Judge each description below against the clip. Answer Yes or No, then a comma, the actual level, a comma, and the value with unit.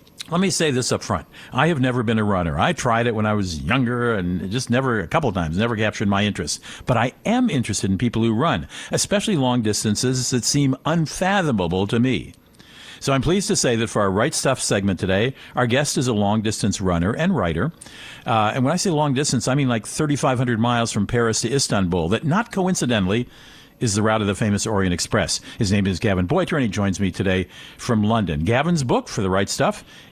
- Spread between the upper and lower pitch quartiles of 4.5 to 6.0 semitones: Yes, average, 4.9 semitones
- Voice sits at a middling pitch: No, low, 120 Hz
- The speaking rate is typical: No, fast, 225 wpm